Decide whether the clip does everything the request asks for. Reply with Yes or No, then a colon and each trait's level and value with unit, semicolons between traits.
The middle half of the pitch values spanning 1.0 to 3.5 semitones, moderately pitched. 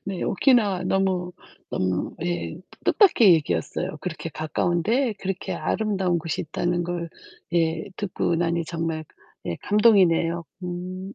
Yes: average, 2.7 semitones; medium, 175 Hz